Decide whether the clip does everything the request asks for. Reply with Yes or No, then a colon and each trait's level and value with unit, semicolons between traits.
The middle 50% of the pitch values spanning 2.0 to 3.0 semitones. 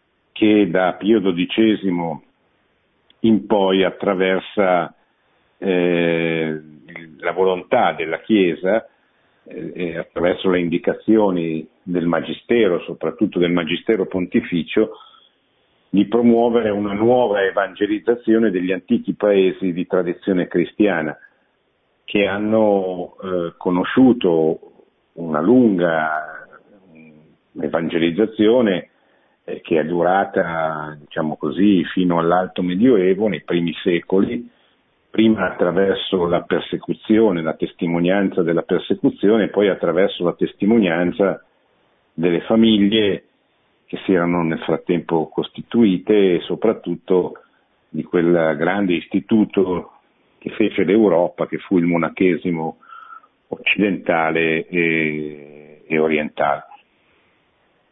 No: average, 3.5 semitones